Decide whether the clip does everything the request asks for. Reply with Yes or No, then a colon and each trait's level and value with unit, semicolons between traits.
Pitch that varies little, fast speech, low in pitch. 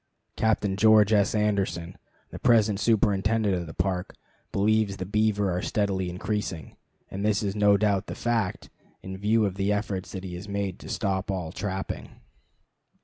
No: narrow, 2.0 semitones; average, 165 wpm; low, 100 Hz